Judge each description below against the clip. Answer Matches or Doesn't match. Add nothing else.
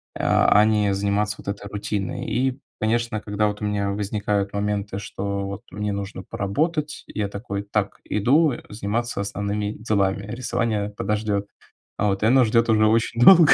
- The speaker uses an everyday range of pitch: Doesn't match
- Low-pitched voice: Matches